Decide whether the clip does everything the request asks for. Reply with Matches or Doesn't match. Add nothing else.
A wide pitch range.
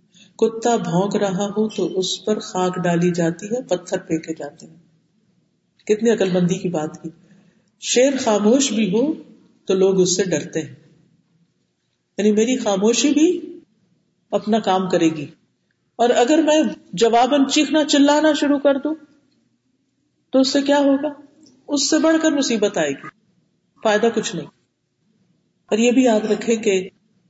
Matches